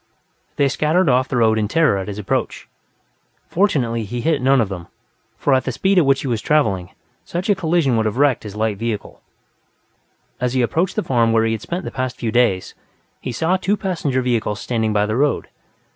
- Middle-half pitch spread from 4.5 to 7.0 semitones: Yes, wide, 5.5 semitones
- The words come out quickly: Yes, fast, 210 wpm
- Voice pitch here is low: Yes, low, 125 Hz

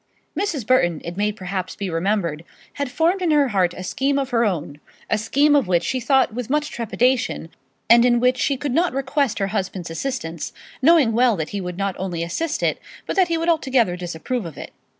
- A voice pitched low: No, high, 235 Hz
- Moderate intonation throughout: No, wide, 7.2 semitones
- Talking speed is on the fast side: Yes, fast, 220 wpm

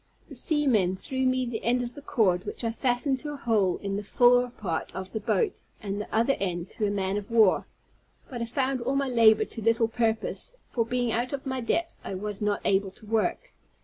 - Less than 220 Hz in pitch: No, high, 230 Hz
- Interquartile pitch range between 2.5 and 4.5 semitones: Yes, average, 3.8 semitones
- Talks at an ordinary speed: No, fast, 225 wpm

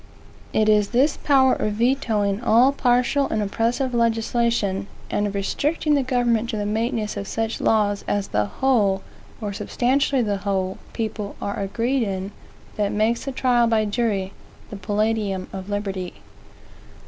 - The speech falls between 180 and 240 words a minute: No, average, 150 wpm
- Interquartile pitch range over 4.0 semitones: No, average, 3.2 semitones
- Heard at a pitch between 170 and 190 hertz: No, high, 220 Hz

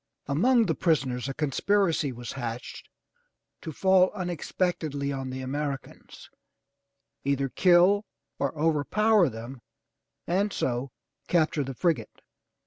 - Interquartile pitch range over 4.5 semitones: Yes, average, 5.2 semitones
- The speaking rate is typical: No, slow, 115 wpm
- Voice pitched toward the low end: No, medium, 150 Hz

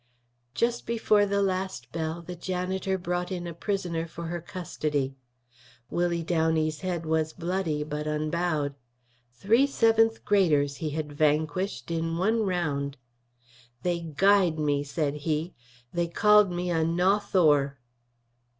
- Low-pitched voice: No, medium, 170 Hz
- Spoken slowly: Yes, slow, 130 wpm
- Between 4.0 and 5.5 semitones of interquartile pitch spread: No, average, 3.6 semitones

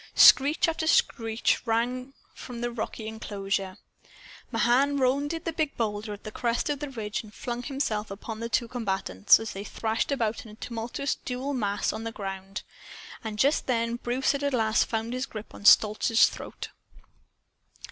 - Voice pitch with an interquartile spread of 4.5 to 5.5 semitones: No, average, 3.3 semitones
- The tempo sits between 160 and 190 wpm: Yes, average, 165 wpm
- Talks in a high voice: Yes, high, 230 Hz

